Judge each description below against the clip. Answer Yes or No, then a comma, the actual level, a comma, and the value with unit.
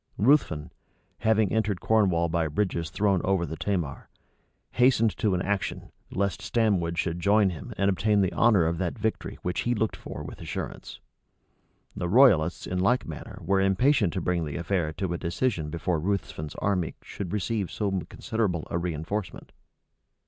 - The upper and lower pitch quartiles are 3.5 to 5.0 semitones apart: Yes, average, 3.8 semitones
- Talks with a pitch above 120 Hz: No, very low, 95 Hz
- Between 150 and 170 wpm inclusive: Yes, average, 165 wpm